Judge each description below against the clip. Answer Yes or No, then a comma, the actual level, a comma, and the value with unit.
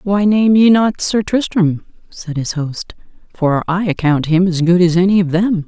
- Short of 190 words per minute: No, average, 200 wpm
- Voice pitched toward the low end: No, medium, 180 Hz